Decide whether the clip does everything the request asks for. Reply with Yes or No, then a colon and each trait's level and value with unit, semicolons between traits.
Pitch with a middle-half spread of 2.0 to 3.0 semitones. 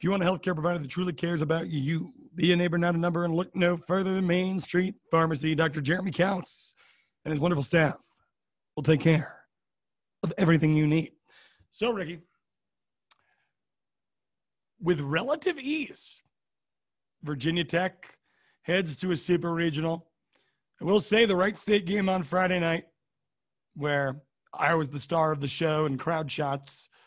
Yes: average, 2.7 semitones